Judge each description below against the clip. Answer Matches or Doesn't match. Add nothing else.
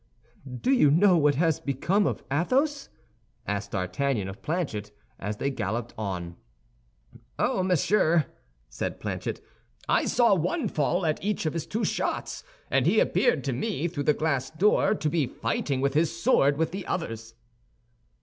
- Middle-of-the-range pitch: Matches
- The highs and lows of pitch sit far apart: Matches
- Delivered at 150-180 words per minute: Matches